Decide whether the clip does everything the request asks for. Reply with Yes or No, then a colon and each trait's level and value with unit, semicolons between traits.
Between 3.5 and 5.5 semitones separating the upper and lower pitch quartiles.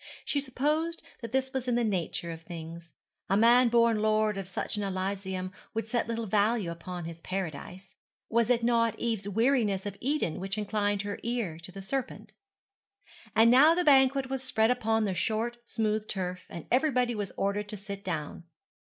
Yes: average, 4.0 semitones